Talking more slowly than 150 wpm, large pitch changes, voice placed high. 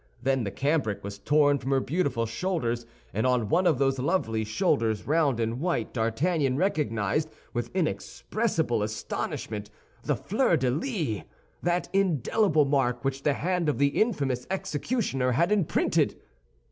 No: average, 140 wpm; wide, 6.4 semitones; low, 135 Hz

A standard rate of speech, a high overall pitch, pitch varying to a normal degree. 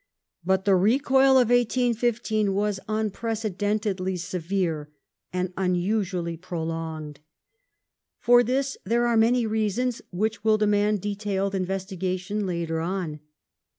No: slow, 110 wpm; high, 200 Hz; average, 3.4 semitones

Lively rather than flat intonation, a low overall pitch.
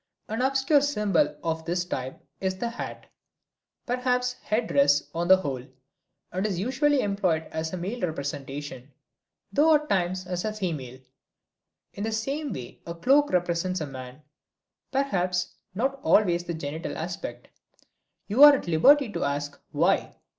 No: wide, 7.7 semitones; medium, 185 Hz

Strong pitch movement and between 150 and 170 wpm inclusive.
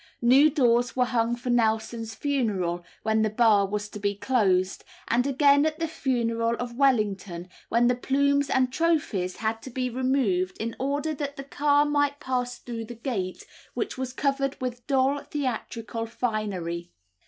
No: average, 3.9 semitones; average, 165 wpm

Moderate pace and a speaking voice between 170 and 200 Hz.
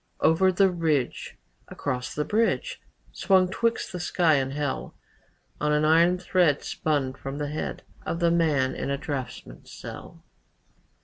No: average, 145 wpm; medium, 155 Hz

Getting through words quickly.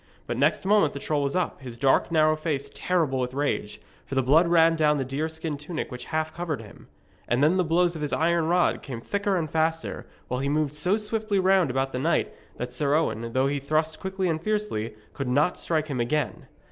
Yes: fast, 225 wpm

